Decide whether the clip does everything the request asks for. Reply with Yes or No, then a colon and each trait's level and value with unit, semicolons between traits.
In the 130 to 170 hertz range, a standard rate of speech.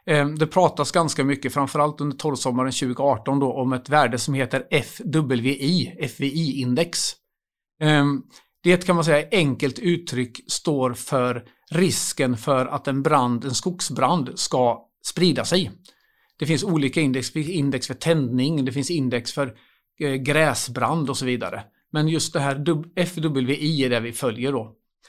Yes: medium, 140 Hz; average, 140 wpm